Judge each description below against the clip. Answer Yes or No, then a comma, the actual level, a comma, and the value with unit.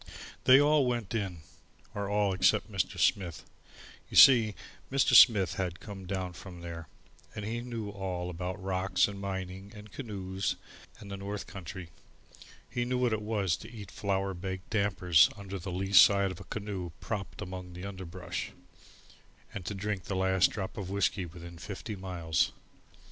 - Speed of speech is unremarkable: Yes, average, 165 wpm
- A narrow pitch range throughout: Yes, narrow, 2.1 semitones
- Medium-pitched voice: No, very low, 95 Hz